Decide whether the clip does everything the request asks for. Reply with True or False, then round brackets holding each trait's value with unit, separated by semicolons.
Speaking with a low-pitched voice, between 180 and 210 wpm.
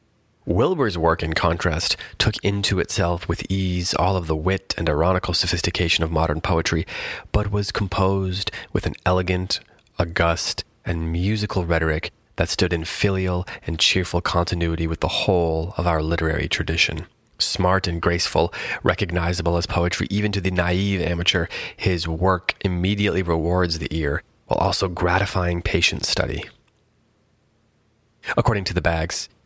False (90 Hz; 140 wpm)